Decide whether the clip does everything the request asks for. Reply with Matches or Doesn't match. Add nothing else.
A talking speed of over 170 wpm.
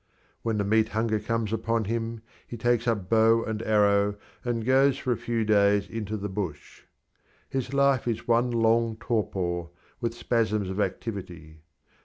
Doesn't match